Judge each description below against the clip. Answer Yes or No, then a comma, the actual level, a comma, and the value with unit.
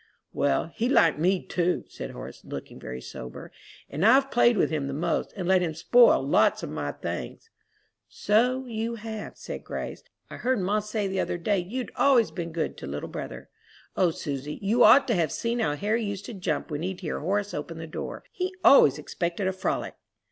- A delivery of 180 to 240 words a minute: Yes, average, 200 wpm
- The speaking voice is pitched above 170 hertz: Yes, high, 190 Hz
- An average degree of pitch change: No, wide, 5.9 semitones